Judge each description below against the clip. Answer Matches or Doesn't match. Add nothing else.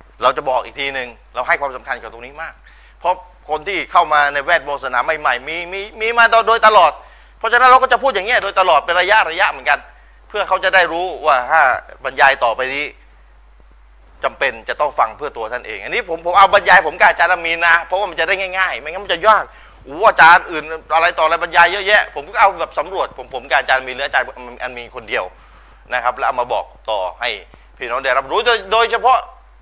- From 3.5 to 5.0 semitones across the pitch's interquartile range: Doesn't match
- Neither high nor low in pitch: Matches